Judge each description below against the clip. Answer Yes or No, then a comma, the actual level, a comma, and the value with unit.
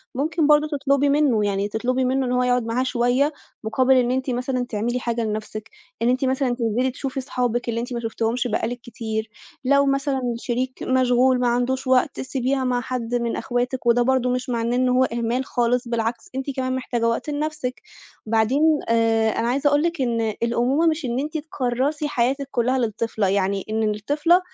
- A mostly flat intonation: Yes, narrow, 2.2 semitones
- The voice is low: No, very high, 250 Hz